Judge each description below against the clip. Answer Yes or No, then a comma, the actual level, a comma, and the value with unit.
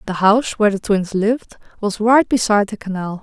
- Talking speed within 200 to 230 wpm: Yes, fast, 205 wpm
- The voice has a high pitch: Yes, high, 210 Hz